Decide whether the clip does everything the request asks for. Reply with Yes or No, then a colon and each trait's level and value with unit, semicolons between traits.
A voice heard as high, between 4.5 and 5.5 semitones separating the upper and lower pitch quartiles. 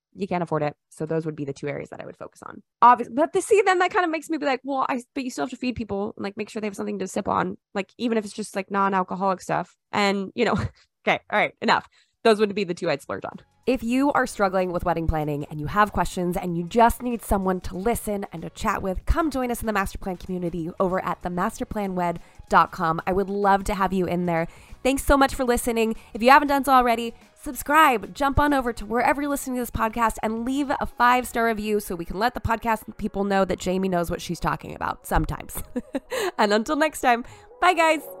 Yes: high, 215 Hz; average, 5.2 semitones